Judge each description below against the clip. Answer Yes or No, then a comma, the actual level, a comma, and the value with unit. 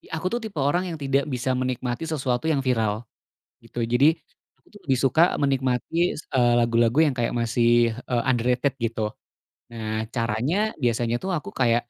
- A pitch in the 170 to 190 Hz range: No, low, 125 Hz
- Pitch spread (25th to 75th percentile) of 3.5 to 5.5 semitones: No, average, 2.7 semitones